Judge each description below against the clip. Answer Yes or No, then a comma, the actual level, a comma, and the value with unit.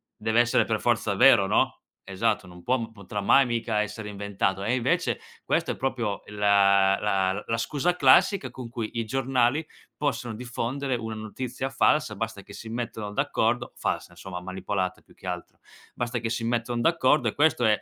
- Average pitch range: Yes, average, 3.2 semitones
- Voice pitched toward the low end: Yes, low, 115 Hz